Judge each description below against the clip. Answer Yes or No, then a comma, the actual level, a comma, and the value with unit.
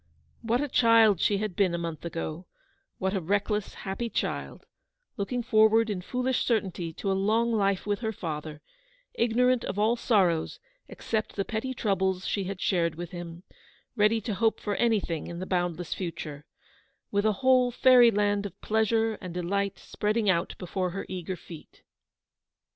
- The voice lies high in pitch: Yes, high, 200 Hz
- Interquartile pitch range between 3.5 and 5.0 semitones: Yes, average, 4.0 semitones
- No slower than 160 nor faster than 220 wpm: Yes, average, 165 wpm